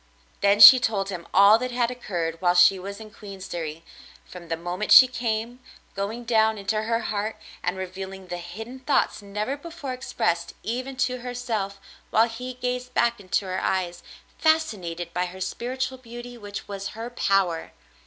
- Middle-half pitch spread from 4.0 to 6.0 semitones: Yes, average, 4.6 semitones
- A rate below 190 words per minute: Yes, average, 165 wpm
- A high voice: Yes, high, 210 Hz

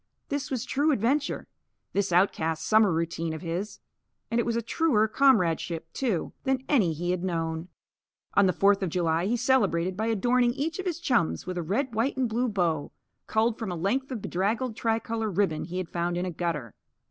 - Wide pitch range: Yes, wide, 5.9 semitones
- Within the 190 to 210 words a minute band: Yes, average, 195 wpm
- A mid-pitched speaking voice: No, high, 205 Hz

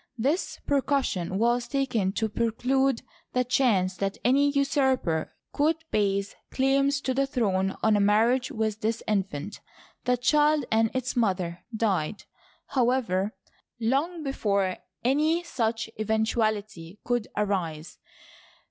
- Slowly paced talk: Yes, slow, 120 wpm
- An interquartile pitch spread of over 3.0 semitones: Yes, average, 5.1 semitones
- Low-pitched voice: No, high, 225 Hz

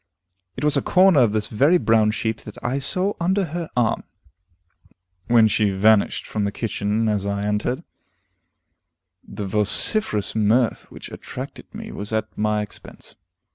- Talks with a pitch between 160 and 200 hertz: No, low, 110 Hz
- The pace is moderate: Yes, average, 150 wpm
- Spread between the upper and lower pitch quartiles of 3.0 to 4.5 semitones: No, average, 4.9 semitones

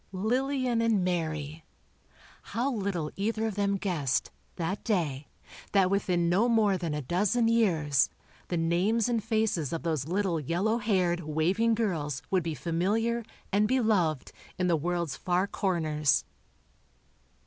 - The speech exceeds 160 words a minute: No, slow, 135 wpm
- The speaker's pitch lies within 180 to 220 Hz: Yes, medium, 185 Hz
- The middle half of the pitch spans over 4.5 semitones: Yes, average, 5.0 semitones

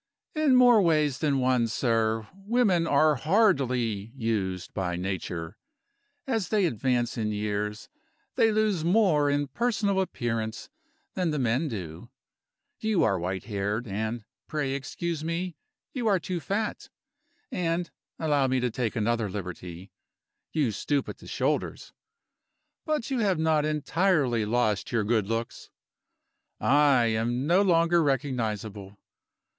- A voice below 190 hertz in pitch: Yes, low, 135 Hz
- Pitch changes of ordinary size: No, wide, 7.7 semitones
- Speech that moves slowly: Yes, slow, 130 wpm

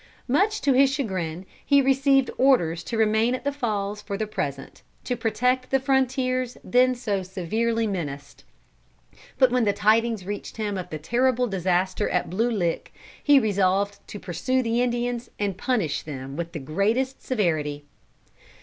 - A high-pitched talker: Yes, high, 220 Hz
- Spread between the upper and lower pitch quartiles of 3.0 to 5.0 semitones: No, wide, 5.6 semitones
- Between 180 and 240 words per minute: No, average, 160 wpm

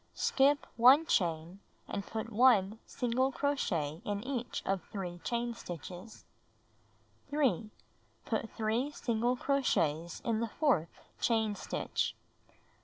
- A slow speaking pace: Yes, slow, 110 wpm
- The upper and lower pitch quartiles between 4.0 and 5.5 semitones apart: Yes, average, 5.1 semitones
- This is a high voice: Yes, high, 225 Hz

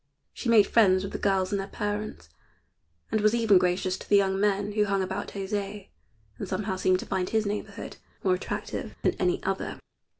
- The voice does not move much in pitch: Yes, narrow, 1.7 semitones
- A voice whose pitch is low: No, high, 200 Hz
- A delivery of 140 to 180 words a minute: No, average, 195 wpm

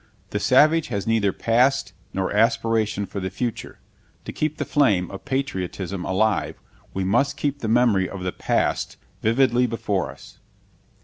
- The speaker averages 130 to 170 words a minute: Yes, average, 150 wpm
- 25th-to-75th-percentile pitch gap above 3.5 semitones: Yes, average, 4.9 semitones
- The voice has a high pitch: No, low, 110 Hz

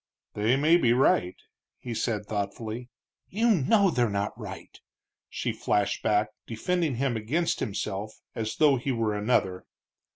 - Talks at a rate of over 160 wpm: No, average, 140 wpm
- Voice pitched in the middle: No, low, 115 Hz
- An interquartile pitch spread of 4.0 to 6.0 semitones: Yes, average, 4.7 semitones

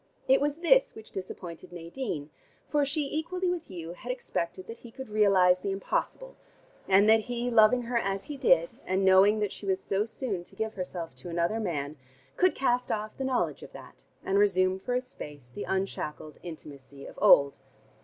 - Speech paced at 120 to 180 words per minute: No, average, 190 wpm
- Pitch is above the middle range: Yes, high, 200 Hz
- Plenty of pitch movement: Yes, wide, 6.0 semitones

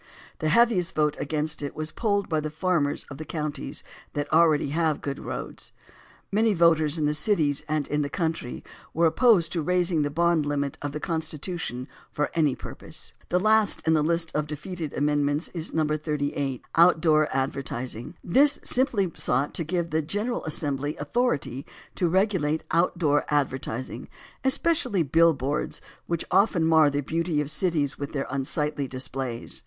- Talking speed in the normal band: Yes, average, 160 wpm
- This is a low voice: No, medium, 155 Hz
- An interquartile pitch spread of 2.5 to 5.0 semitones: Yes, average, 2.9 semitones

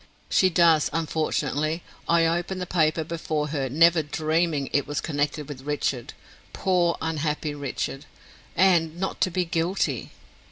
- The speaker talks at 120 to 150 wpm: Yes, slow, 135 wpm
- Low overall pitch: No, medium, 160 Hz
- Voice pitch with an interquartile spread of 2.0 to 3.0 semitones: Yes, narrow, 2.4 semitones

